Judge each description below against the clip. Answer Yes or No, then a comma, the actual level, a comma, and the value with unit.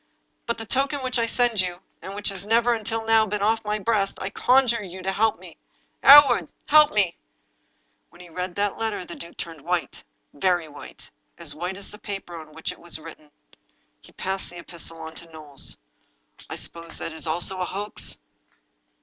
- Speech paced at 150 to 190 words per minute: No, fast, 205 wpm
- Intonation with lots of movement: No, average, 4.8 semitones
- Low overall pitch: No, high, 190 Hz